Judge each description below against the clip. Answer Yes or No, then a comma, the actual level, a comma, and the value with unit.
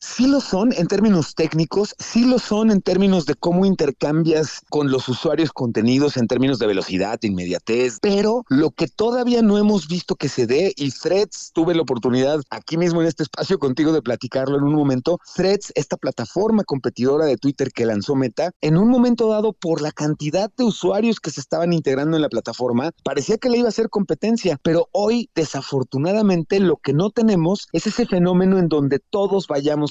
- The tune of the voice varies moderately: No, wide, 6.4 semitones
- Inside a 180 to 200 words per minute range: Yes, fast, 190 wpm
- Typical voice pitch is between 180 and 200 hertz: No, medium, 165 Hz